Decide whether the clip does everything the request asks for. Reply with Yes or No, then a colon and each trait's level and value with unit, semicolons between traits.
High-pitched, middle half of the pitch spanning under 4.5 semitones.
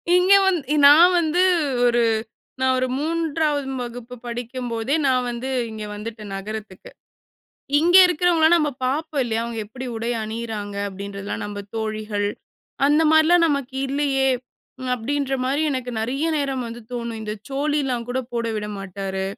No: very high, 250 Hz; average, 4.8 semitones